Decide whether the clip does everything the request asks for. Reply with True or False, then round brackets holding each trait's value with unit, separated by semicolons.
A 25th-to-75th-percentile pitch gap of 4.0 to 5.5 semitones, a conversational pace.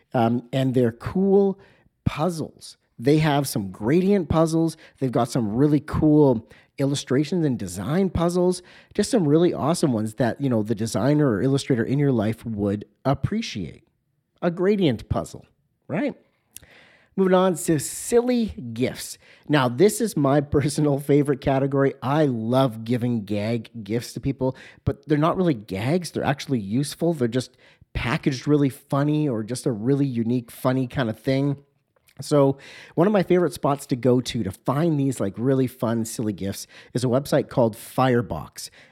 True (4.5 semitones; 160 wpm)